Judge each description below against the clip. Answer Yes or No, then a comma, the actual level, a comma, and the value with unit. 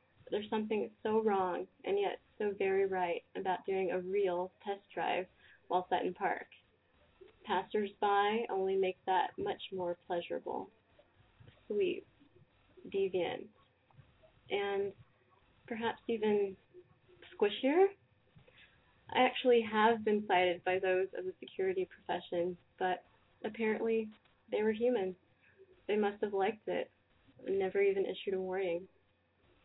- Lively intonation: Yes, wide, 6.5 semitones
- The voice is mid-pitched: No, high, 210 Hz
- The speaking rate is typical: No, slow, 120 wpm